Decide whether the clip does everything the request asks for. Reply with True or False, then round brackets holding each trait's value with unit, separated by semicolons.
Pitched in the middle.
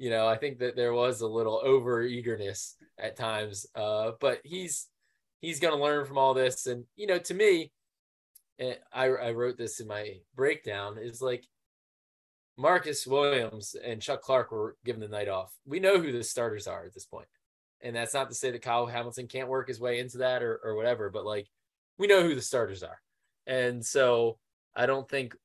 False (125 Hz)